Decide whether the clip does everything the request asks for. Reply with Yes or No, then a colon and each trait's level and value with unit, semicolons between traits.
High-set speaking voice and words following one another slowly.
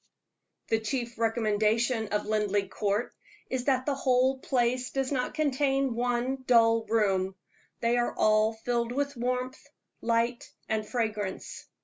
Yes: high, 235 Hz; slow, 130 wpm